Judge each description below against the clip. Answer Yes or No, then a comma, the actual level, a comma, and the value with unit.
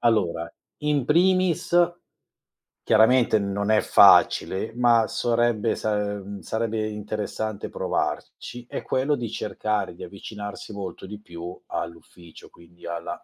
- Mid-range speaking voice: No, low, 110 Hz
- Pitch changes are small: No, average, 3.2 semitones